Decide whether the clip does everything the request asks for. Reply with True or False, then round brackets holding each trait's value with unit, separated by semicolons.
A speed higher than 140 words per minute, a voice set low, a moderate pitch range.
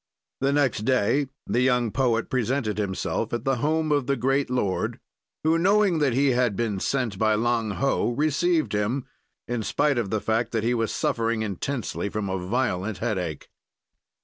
True (175 wpm; 120 Hz; 4.2 semitones)